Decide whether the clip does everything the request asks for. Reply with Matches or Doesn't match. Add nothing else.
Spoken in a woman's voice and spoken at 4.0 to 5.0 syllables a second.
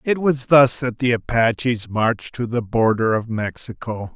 Doesn't match